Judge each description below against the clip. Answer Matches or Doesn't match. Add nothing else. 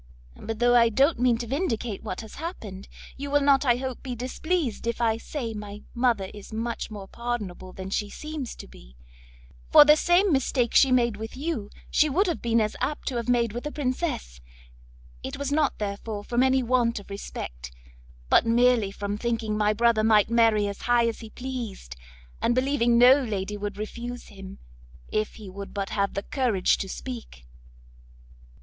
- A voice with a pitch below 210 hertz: Doesn't match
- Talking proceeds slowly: Doesn't match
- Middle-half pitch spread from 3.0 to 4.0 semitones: Matches